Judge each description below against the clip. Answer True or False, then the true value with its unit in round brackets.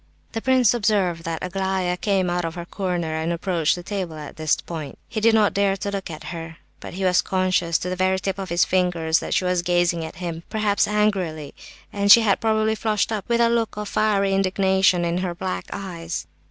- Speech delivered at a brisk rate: True (220 wpm)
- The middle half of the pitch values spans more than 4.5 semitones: False (2.8 semitones)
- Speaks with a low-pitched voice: False (185 Hz)